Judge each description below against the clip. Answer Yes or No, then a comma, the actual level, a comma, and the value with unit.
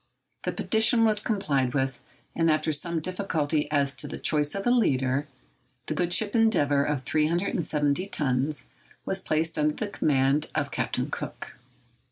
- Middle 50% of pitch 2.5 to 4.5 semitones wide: No, average, 5.1 semitones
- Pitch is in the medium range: Yes, medium, 155 Hz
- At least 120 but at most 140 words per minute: No, average, 155 wpm